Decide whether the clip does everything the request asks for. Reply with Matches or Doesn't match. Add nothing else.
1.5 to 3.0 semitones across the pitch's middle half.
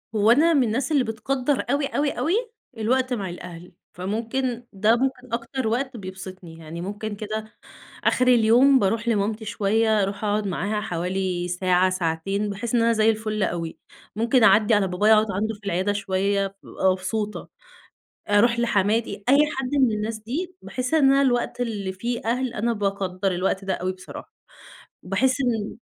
Doesn't match